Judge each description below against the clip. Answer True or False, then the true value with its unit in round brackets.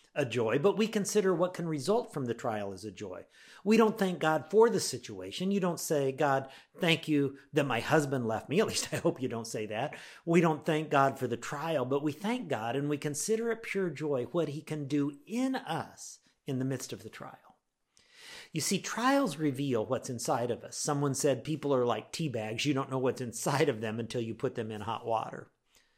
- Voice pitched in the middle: True (145 Hz)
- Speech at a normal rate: False (225 wpm)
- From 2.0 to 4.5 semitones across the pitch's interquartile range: False (5.6 semitones)